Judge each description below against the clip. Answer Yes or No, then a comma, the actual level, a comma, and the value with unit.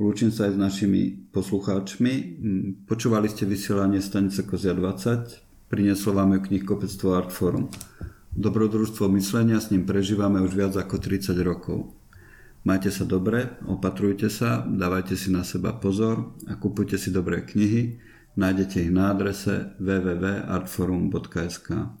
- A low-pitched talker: Yes, low, 100 Hz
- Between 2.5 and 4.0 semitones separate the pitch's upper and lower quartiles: No, narrow, 1.8 semitones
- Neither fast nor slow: Yes, average, 130 wpm